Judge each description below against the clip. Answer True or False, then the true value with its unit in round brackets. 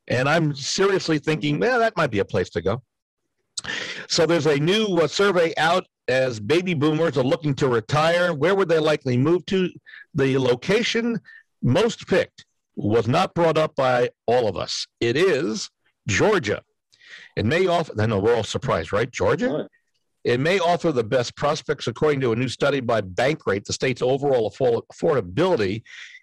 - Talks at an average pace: True (170 wpm)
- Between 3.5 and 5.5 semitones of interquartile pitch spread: True (5.2 semitones)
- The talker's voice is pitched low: False (155 Hz)